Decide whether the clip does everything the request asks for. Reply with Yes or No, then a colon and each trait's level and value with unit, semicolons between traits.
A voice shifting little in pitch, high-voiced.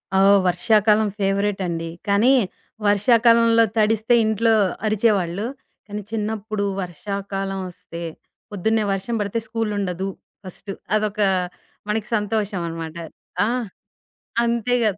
Yes: narrow, 2.3 semitones; high, 210 Hz